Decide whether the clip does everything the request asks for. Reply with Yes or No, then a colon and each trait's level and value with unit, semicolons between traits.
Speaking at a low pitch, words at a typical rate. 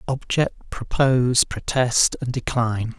No: low, 125 Hz; slow, 100 wpm